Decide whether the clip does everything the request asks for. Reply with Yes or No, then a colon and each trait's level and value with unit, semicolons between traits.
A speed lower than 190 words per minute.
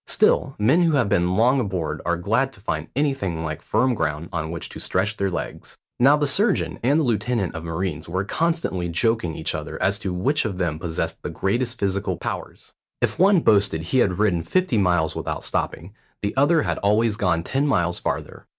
No: average, 200 wpm